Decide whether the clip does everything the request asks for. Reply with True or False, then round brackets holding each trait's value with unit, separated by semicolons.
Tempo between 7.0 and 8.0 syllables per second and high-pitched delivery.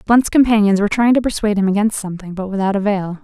True (7.1 syllables/s; 205 Hz)